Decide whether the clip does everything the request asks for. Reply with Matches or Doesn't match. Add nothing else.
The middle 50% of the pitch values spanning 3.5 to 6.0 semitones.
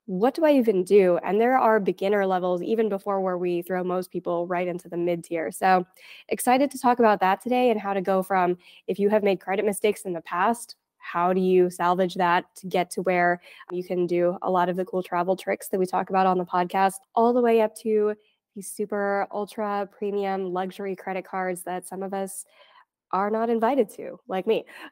Doesn't match